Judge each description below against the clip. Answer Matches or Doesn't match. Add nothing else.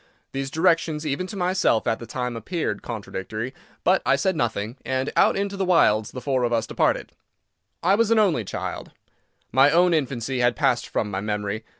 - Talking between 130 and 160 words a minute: Doesn't match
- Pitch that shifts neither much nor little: Doesn't match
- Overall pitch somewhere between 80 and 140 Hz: Matches